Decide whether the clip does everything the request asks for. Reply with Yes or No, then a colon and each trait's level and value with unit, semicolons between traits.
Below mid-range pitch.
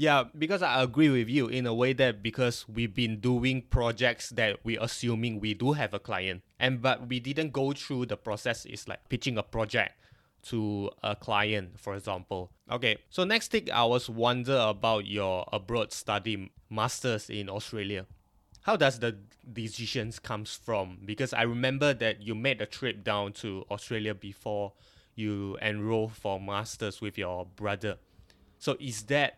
Yes: low, 110 Hz